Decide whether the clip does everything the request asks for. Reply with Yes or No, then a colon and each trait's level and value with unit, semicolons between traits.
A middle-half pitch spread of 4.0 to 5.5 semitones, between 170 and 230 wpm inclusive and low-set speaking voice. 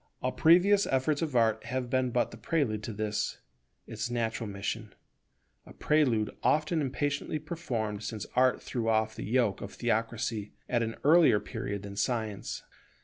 No: average, 4.6 semitones; average, 155 wpm; low, 120 Hz